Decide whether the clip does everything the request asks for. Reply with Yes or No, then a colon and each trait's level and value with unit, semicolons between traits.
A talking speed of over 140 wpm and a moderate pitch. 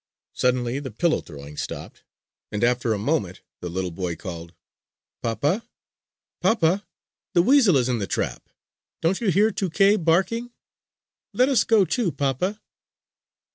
No: slow, 135 wpm; medium, 145 Hz